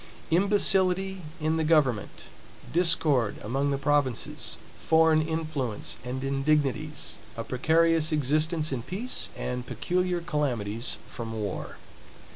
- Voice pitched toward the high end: No, medium, 150 Hz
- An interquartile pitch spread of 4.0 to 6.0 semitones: Yes, average, 4.4 semitones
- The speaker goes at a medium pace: No, slow, 105 wpm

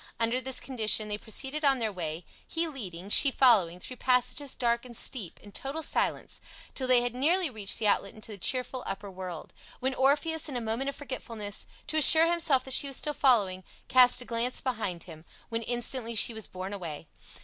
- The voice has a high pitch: Yes, high, 240 Hz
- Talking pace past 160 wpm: Yes, average, 200 wpm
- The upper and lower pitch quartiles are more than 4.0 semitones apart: Yes, average, 4.7 semitones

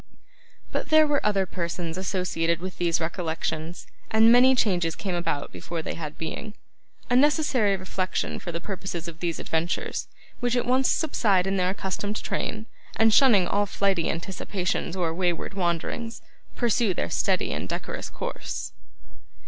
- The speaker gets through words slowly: No, average, 150 wpm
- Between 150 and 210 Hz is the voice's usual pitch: Yes, medium, 185 Hz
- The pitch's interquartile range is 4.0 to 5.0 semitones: Yes, average, 4.5 semitones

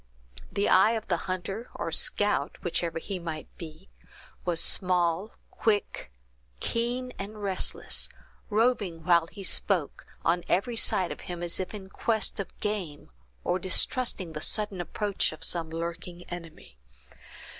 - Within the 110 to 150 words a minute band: Yes, average, 140 wpm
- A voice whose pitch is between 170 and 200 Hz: Yes, medium, 185 Hz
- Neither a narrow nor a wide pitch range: Yes, average, 3.6 semitones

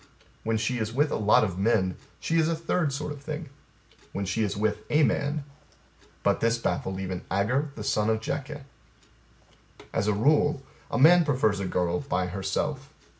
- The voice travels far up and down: Yes, wide, 6.7 semitones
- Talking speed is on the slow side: No, average, 180 wpm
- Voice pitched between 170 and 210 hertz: No, low, 115 Hz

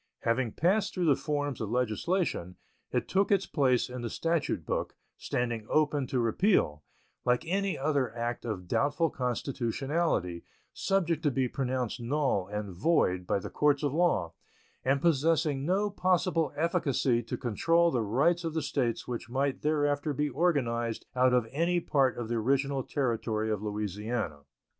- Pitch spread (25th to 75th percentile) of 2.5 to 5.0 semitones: No, wide, 5.4 semitones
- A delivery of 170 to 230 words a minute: No, average, 155 wpm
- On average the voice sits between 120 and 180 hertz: Yes, low, 135 Hz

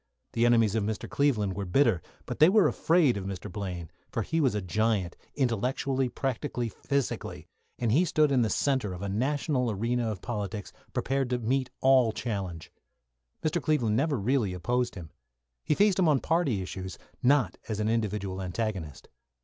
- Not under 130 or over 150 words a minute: No, average, 175 wpm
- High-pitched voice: No, low, 115 Hz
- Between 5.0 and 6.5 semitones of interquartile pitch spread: Yes, average, 5.3 semitones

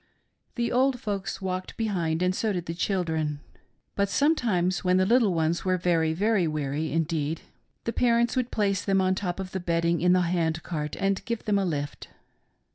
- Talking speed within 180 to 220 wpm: Yes, average, 190 wpm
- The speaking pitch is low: No, medium, 185 Hz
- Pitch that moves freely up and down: No, average, 3.7 semitones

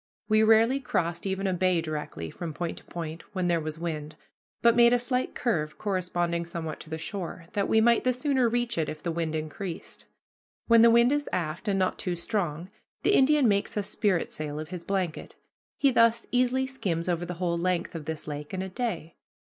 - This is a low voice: No, medium, 185 Hz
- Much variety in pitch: Yes, wide, 5.8 semitones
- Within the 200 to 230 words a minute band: Yes, fast, 205 wpm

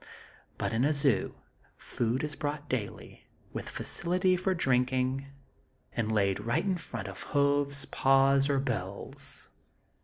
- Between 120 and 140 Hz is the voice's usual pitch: Yes, low, 135 Hz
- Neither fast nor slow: No, slow, 130 wpm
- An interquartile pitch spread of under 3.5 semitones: No, average, 3.8 semitones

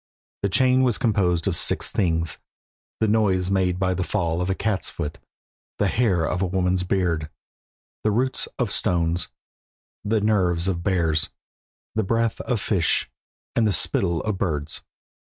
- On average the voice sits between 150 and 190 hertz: No, very low, 95 Hz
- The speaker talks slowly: No, average, 155 wpm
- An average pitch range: Yes, average, 3.7 semitones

